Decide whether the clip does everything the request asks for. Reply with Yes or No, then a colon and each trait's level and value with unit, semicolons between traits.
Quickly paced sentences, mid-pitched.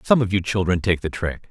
No: fast, 280 wpm; very low, 95 Hz